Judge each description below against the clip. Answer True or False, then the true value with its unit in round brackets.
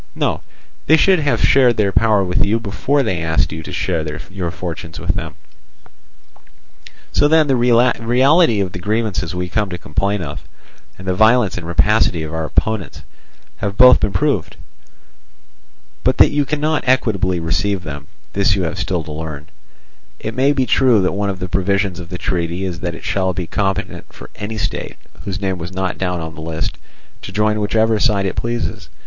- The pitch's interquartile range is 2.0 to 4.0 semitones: False (4.4 semitones)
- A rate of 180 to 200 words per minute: True (190 wpm)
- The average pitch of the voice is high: False (95 Hz)